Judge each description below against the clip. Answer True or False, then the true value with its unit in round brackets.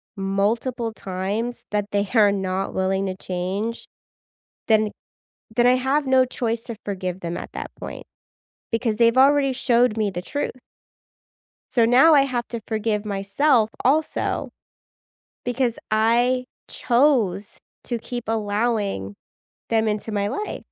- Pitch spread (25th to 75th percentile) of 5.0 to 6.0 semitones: False (3.6 semitones)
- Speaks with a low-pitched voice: False (225 Hz)